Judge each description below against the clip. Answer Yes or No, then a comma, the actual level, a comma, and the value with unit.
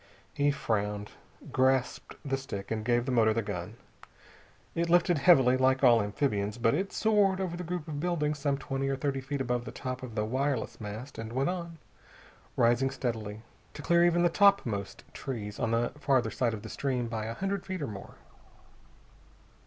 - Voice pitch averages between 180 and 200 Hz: No, low, 130 Hz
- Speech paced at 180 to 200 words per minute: Yes, average, 185 wpm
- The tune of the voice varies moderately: Yes, average, 4.9 semitones